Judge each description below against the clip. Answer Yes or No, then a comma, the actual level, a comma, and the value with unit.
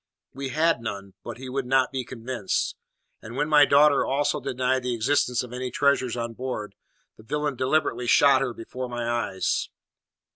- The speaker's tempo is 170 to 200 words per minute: Yes, average, 175 wpm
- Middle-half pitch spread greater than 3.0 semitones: No, narrow, 2.6 semitones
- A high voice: No, low, 130 Hz